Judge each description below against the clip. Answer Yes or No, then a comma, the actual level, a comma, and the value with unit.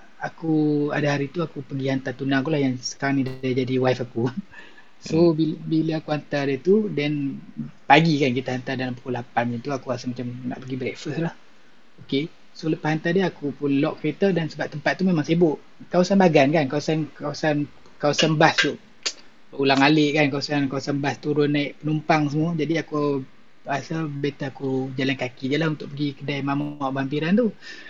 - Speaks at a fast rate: Yes, fast, 195 wpm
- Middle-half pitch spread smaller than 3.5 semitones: Yes, average, 2.8 semitones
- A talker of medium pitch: Yes, medium, 145 Hz